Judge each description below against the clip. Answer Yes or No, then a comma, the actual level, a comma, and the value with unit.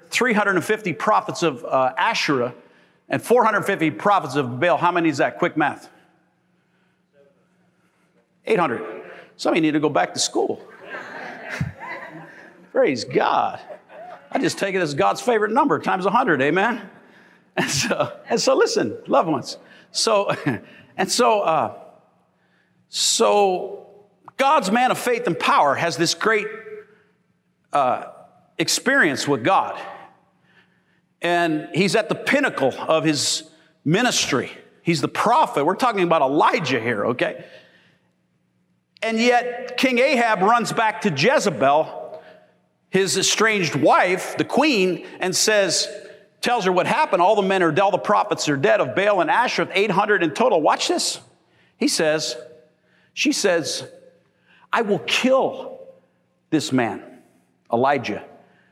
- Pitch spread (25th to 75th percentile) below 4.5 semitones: No, average, 5.1 semitones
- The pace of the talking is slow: Yes, slow, 130 wpm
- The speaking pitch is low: No, medium, 185 Hz